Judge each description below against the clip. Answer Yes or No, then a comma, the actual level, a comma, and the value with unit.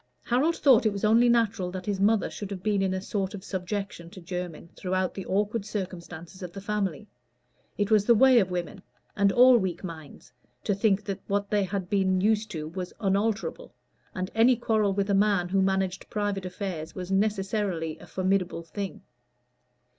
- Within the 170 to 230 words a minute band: Yes, average, 185 wpm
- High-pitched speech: Yes, high, 195 Hz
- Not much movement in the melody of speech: Yes, narrow, 2.3 semitones